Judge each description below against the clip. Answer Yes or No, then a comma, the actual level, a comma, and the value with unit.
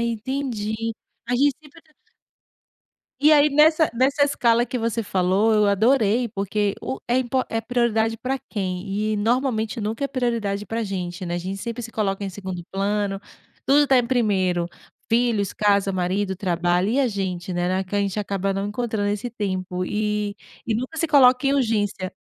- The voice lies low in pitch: No, high, 215 Hz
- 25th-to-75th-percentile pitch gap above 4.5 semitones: No, average, 4.1 semitones